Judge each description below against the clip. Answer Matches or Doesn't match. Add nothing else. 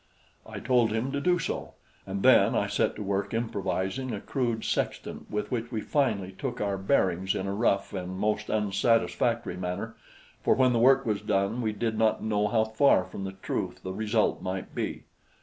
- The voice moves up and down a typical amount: Matches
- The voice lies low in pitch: Matches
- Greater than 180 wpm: Matches